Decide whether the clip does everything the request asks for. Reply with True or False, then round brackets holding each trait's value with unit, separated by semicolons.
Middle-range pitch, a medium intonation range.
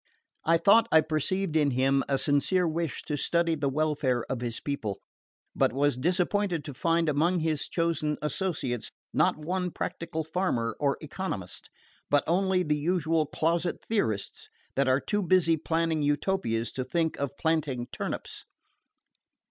True (155 Hz; 3.5 semitones)